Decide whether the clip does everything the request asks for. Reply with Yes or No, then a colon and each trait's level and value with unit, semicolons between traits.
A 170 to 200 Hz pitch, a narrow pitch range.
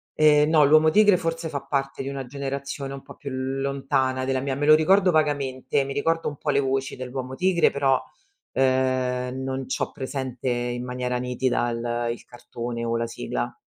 No: low, 135 Hz; narrow, 2.1 semitones